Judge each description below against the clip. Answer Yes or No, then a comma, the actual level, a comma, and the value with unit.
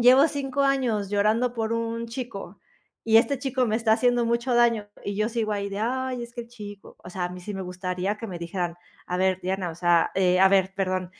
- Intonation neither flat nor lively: Yes, average, 4.2 semitones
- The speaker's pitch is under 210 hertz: No, high, 215 Hz